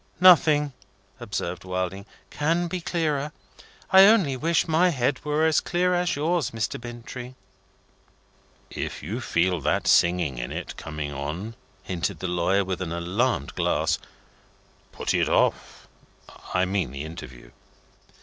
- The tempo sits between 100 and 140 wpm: Yes, slow, 135 wpm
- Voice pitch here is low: Yes, low, 115 Hz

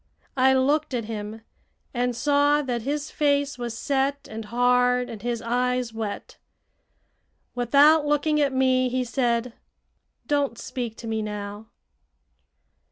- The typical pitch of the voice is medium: No, very high, 250 Hz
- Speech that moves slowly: Yes, slow, 130 wpm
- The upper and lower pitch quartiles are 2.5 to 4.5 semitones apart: Yes, average, 3.4 semitones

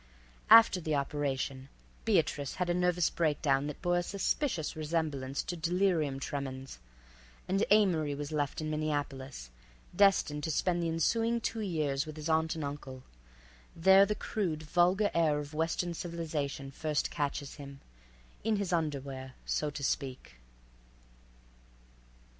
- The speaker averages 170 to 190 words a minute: No, slow, 135 wpm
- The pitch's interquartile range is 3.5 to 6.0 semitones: Yes, average, 3.8 semitones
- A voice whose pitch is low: No, medium, 155 Hz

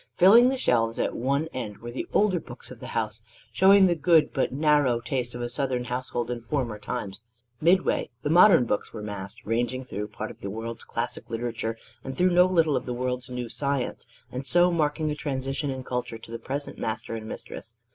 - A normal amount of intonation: Yes, average, 4.5 semitones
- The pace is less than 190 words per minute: No, fast, 205 wpm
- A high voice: No, low, 130 Hz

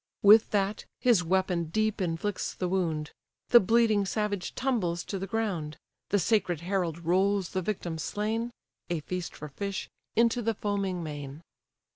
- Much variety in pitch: No, average, 3.7 semitones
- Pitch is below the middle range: No, high, 190 Hz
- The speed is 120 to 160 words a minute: Yes, average, 150 wpm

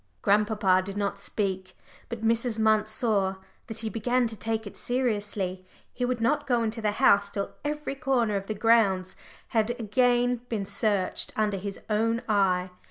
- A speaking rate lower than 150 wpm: No, average, 165 wpm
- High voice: Yes, high, 215 Hz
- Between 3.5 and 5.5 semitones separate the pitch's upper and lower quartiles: No, average, 2.8 semitones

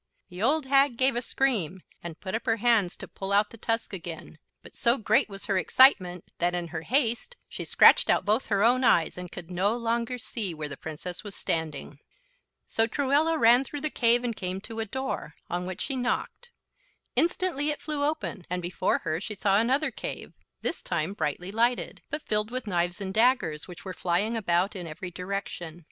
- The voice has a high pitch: Yes, high, 210 Hz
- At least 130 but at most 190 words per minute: No, average, 200 wpm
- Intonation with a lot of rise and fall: Yes, wide, 5.7 semitones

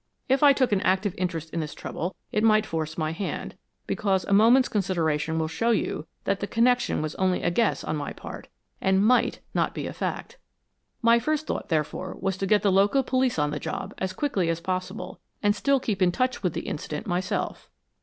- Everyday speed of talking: No, fast, 210 wpm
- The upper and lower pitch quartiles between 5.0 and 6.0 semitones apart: Yes, wide, 5.4 semitones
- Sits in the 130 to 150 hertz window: No, high, 190 Hz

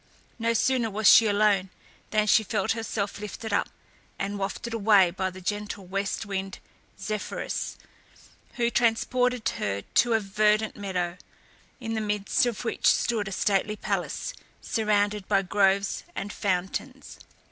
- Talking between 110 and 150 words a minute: Yes, average, 140 wpm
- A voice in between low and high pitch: No, high, 210 Hz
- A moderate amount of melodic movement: No, narrow, 2.3 semitones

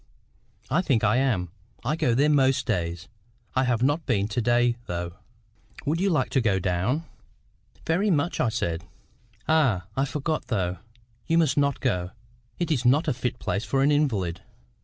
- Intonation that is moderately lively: No, wide, 6.5 semitones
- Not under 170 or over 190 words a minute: Yes, average, 175 wpm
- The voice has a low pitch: Yes, low, 125 Hz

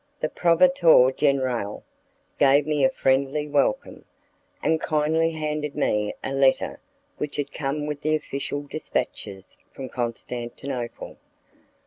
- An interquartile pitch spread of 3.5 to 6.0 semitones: No, narrow, 2.6 semitones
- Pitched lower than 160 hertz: Yes, medium, 140 Hz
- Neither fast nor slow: No, slow, 115 wpm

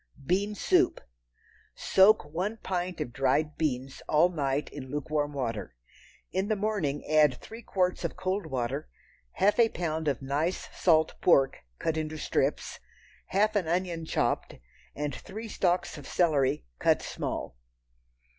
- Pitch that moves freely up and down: No, average, 4.7 semitones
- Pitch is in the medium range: Yes, medium, 160 Hz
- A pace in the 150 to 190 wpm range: No, average, 140 wpm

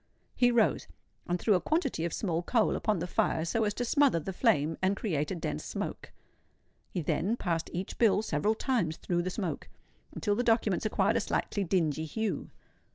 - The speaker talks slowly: No, average, 190 wpm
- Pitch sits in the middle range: No, high, 195 Hz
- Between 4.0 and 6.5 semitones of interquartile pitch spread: Yes, average, 4.8 semitones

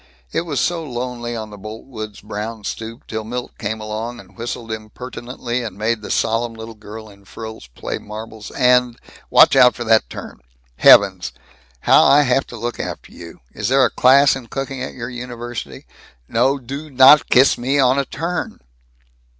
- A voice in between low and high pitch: No, low, 120 Hz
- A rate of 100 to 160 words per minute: No, average, 175 wpm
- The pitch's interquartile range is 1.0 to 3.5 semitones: Yes, average, 2.8 semitones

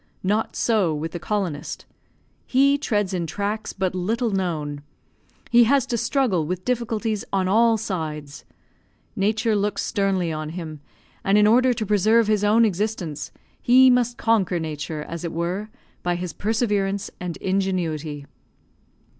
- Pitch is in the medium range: No, high, 195 Hz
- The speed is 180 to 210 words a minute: No, average, 145 wpm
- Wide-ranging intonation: No, average, 4.5 semitones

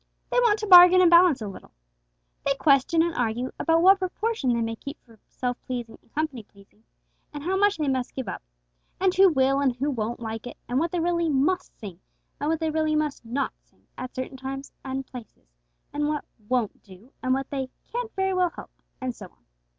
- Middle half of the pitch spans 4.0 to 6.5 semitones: Yes, wide, 5.6 semitones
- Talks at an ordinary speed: No, fast, 215 wpm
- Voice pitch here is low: No, very high, 275 Hz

